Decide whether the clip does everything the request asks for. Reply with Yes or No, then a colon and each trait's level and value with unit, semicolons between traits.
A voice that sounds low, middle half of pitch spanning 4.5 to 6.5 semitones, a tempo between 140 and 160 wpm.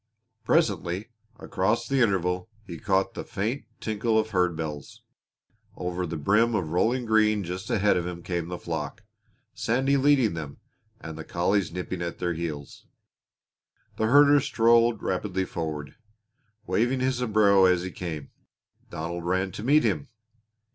Yes: very low, 95 Hz; average, 4.8 semitones; average, 150 wpm